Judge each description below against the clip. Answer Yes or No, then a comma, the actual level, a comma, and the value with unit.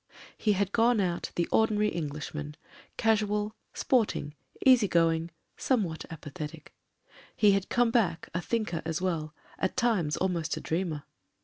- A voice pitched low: No, medium, 185 Hz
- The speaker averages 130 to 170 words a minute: Yes, average, 145 wpm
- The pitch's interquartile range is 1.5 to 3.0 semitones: No, average, 4.9 semitones